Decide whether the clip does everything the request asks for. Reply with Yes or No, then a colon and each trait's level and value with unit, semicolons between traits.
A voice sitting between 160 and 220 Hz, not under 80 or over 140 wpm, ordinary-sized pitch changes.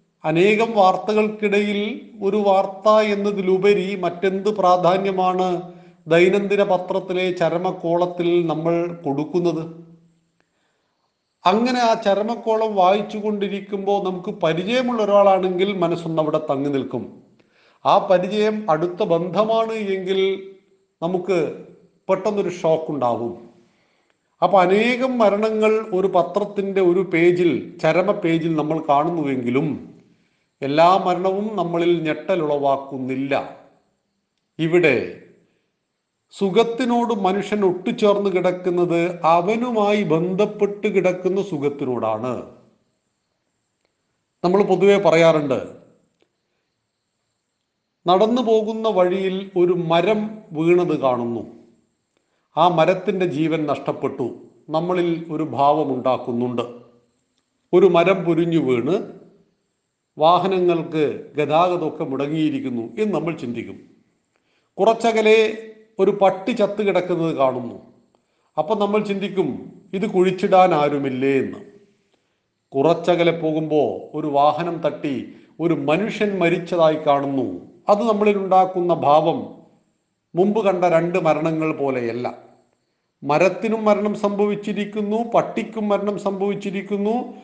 Yes: medium, 185 Hz; average, 85 wpm; average, 4.2 semitones